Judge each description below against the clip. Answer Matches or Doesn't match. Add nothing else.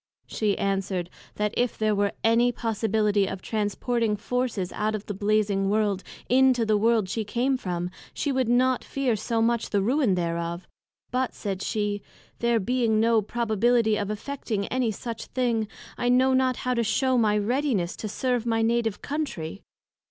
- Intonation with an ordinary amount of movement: Matches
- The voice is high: Matches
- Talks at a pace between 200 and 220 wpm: Doesn't match